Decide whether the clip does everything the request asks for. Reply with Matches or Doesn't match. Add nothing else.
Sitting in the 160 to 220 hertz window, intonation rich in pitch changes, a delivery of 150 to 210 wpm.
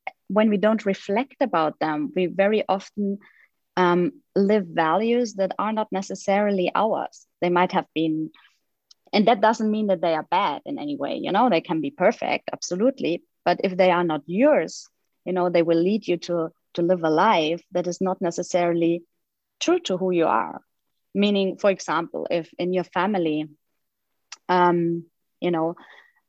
Doesn't match